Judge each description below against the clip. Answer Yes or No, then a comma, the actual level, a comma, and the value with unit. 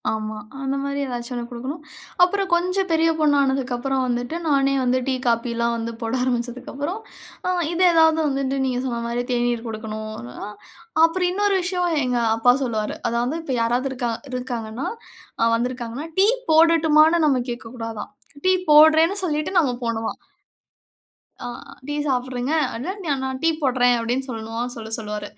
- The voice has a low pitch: No, very high, 255 Hz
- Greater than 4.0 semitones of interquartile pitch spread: Yes, average, 4.6 semitones